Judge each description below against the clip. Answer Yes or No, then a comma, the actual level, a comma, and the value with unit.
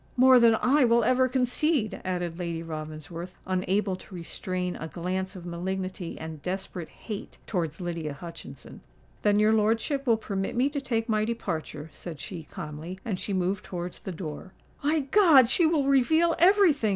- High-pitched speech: Yes, high, 195 Hz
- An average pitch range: No, wide, 6.3 semitones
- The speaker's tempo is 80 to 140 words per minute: No, average, 170 wpm